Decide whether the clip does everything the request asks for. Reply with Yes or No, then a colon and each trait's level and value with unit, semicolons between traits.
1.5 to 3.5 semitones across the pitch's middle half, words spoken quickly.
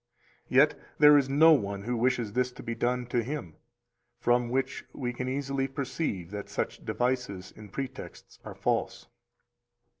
No: average, 2.9 semitones; average, 155 wpm